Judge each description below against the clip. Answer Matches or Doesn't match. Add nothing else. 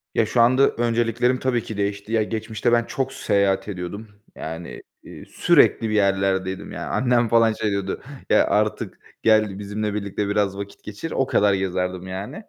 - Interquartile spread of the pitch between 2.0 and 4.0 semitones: Matches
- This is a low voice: Matches